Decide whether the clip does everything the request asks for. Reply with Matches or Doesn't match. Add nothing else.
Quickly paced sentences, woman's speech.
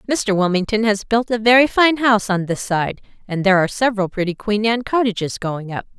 Matches